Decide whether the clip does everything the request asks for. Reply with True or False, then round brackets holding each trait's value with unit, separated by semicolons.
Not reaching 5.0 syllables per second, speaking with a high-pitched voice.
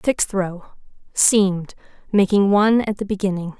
True (4.8 syllables/s; 195 Hz)